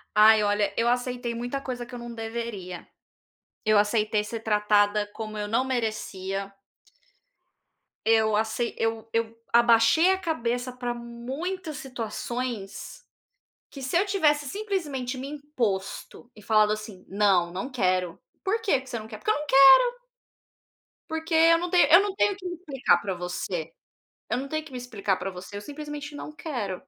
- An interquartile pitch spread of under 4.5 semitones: No, wide, 5.6 semitones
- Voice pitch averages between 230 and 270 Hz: Yes, high, 235 Hz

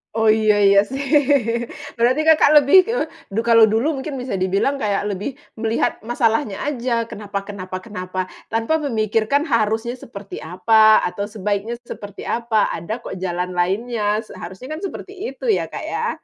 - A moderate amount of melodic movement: Yes, average, 3.3 semitones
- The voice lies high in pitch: Yes, high, 220 Hz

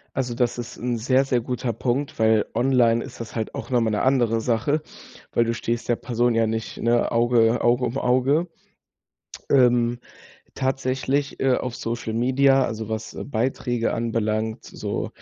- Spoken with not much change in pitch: Yes, narrow, 2.0 semitones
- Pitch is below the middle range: Yes, low, 120 Hz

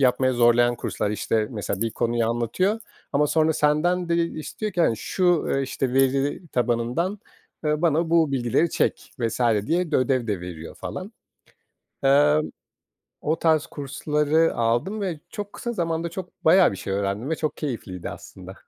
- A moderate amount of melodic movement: No, wide, 5.9 semitones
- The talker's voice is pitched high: No, medium, 145 Hz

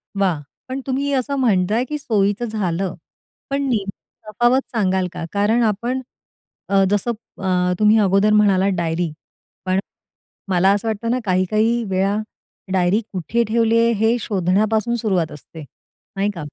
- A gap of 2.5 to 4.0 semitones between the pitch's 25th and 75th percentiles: Yes, average, 3.7 semitones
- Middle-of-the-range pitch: No, high, 205 Hz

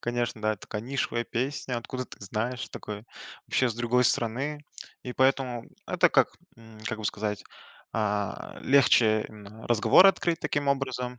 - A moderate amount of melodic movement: Yes, average, 3.2 semitones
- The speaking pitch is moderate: No, low, 120 Hz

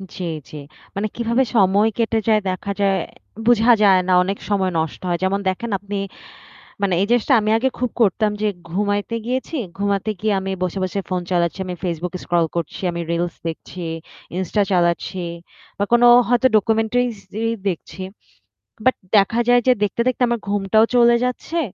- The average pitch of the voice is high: Yes, high, 205 Hz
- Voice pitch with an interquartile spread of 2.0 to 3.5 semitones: No, average, 3.9 semitones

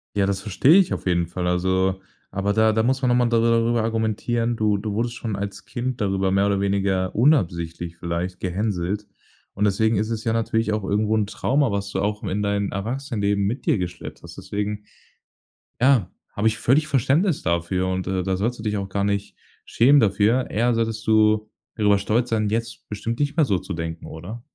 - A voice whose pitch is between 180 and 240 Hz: No, low, 105 Hz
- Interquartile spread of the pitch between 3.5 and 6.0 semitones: No, average, 3.0 semitones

